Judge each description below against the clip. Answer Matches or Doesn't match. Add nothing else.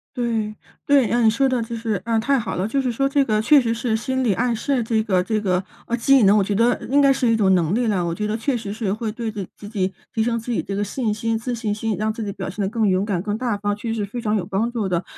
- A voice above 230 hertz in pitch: Doesn't match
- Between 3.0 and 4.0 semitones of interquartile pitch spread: Doesn't match